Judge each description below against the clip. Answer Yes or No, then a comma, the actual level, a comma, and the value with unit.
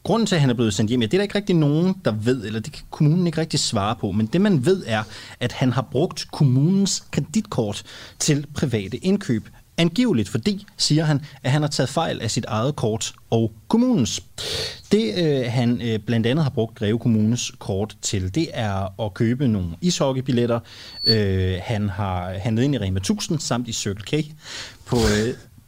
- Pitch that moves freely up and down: Yes, wide, 5.9 semitones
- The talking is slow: No, average, 200 wpm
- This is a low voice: Yes, low, 125 Hz